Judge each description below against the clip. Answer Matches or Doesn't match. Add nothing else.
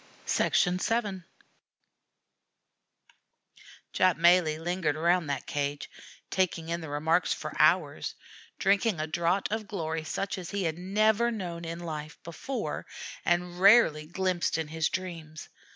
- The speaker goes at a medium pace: Doesn't match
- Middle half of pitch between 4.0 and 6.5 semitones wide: Doesn't match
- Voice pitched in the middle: Matches